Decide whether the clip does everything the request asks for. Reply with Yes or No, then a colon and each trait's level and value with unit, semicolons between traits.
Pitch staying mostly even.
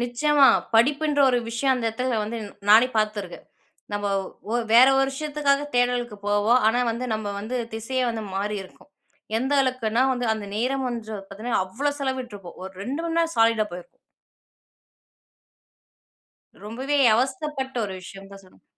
No: average, 3.7 semitones